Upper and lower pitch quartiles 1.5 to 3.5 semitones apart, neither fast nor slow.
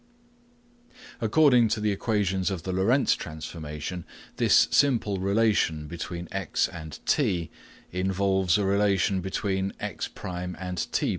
No: average, 2.8 semitones; slow, 120 wpm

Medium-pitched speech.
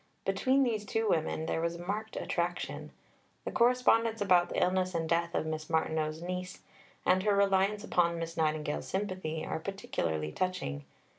Yes: medium, 180 Hz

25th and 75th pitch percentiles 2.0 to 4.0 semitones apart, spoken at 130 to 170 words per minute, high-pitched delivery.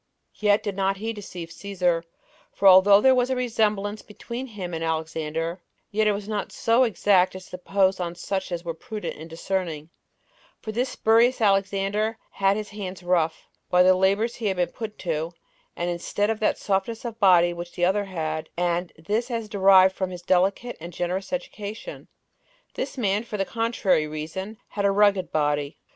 No: average, 3.3 semitones; average, 185 wpm; high, 195 Hz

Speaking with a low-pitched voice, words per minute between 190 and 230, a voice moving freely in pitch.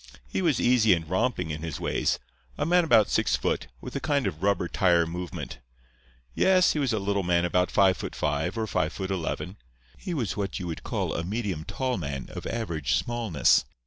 Yes: very low, 95 Hz; fast, 205 wpm; wide, 5.9 semitones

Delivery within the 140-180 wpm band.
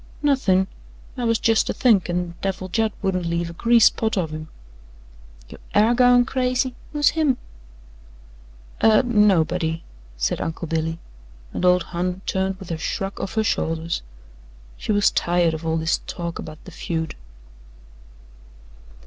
Yes: average, 145 wpm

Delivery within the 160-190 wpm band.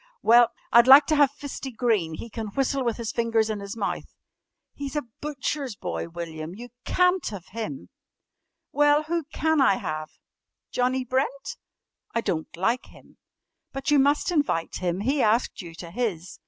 Yes: average, 170 wpm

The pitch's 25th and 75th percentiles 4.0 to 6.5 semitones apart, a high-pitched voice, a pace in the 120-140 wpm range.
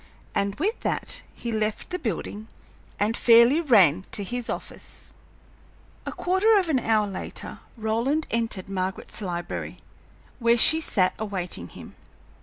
Yes: average, 4.9 semitones; high, 220 Hz; slow, 135 wpm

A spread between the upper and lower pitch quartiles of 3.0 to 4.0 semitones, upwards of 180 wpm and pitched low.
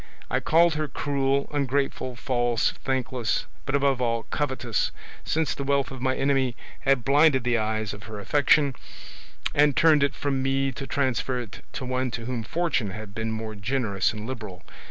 No: average, 3.6 semitones; average, 175 wpm; low, 130 Hz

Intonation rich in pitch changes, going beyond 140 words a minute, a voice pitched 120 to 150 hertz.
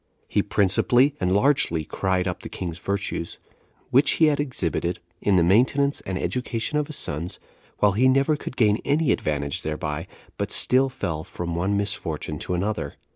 No: wide, 7.3 semitones; average, 170 wpm; low, 100 Hz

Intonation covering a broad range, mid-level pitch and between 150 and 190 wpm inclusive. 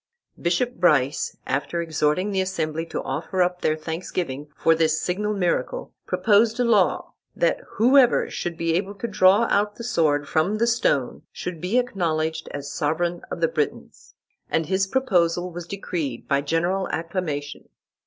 No: average, 4.1 semitones; medium, 175 Hz; average, 155 wpm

